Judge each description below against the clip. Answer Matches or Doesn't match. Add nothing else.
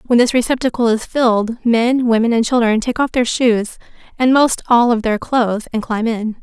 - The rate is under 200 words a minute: Doesn't match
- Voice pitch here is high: Matches